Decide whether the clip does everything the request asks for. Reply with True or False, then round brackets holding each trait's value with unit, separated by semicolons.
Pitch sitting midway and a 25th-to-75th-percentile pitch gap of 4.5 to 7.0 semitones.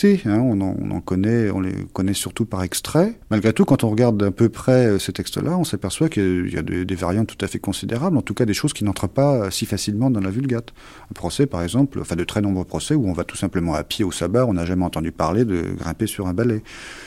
False (105 Hz; 5.0 semitones)